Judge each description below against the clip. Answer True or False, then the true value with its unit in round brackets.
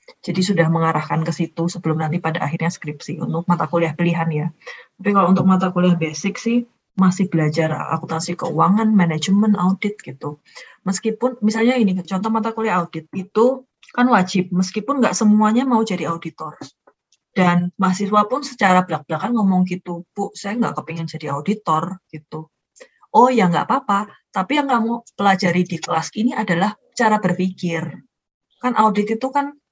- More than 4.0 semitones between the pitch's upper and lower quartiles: True (4.8 semitones)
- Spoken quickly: True (155 wpm)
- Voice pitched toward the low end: False (190 Hz)